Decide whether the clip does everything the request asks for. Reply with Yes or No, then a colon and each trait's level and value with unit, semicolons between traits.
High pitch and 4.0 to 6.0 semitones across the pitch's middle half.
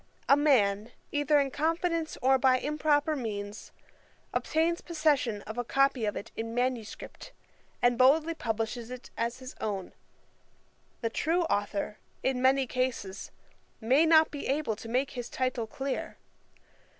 Yes: very high, 255 Hz; average, 4.4 semitones